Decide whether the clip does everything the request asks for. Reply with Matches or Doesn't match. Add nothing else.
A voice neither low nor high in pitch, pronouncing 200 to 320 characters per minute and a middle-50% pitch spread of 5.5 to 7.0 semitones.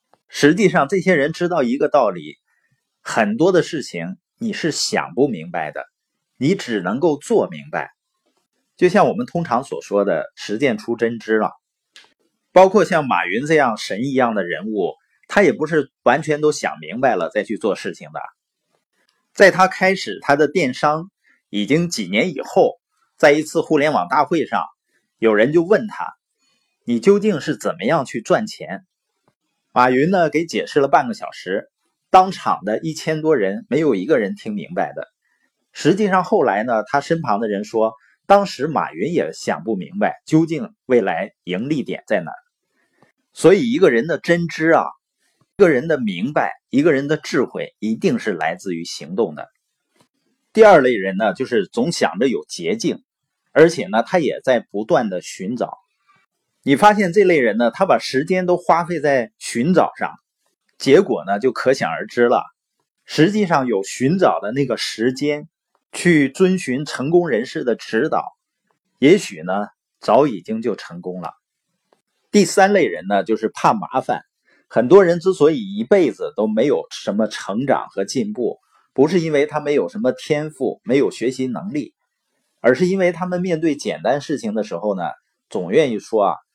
Matches